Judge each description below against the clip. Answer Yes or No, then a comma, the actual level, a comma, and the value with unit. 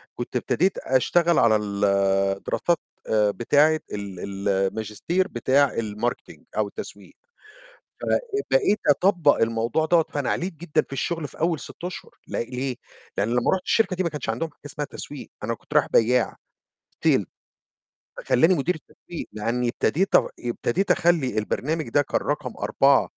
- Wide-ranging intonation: Yes, wide, 6.9 semitones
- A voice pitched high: No, low, 130 Hz